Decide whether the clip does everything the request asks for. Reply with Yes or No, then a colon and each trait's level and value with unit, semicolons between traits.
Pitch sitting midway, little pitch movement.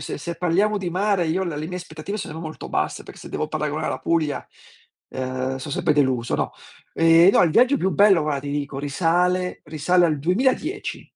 No: medium, 165 Hz; average, 3.9 semitones